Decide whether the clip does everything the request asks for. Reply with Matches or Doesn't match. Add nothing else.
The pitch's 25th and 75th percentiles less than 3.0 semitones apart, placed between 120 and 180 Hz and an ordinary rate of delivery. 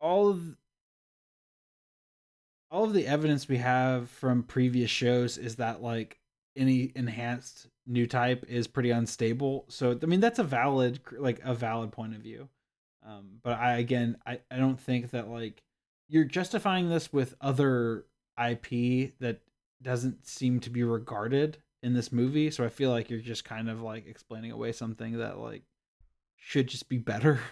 Matches